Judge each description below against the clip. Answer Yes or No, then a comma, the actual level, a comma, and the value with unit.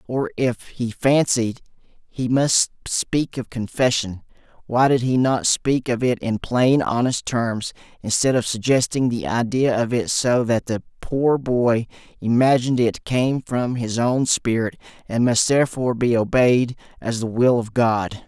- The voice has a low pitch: Yes, low, 120 Hz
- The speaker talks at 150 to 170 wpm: Yes, average, 160 wpm